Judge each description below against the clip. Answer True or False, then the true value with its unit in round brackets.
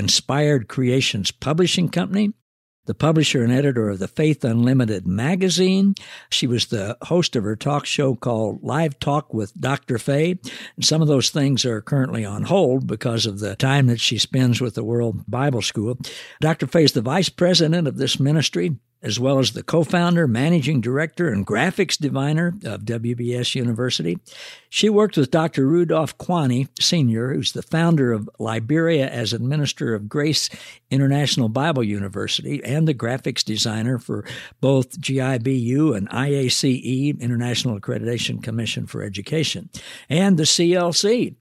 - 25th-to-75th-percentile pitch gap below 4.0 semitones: False (4.9 semitones)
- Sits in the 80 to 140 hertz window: True (135 Hz)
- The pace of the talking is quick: False (155 wpm)